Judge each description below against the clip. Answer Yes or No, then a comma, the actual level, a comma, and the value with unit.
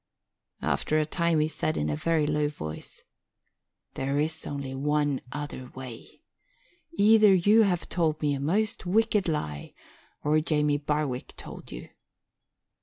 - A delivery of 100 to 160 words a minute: Yes, average, 140 wpm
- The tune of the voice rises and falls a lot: No, average, 3.1 semitones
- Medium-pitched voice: Yes, medium, 150 Hz